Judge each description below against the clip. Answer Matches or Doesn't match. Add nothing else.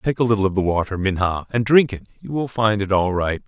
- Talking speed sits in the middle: Doesn't match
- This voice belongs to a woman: Doesn't match